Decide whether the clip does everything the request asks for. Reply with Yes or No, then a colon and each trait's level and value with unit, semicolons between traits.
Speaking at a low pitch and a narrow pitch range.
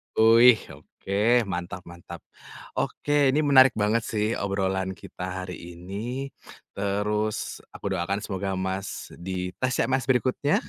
No: low, 100 Hz; average, 3.8 semitones